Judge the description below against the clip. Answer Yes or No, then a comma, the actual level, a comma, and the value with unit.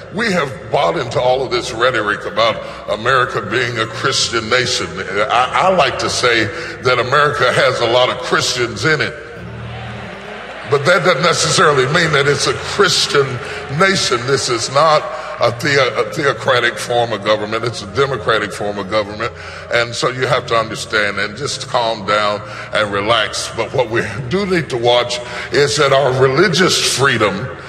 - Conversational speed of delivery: Yes, average, 170 wpm